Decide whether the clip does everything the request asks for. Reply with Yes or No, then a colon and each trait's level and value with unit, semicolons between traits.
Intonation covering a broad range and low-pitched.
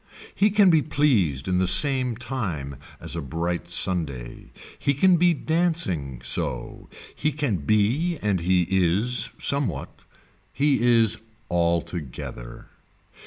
Yes: wide, 9.0 semitones; low, 105 Hz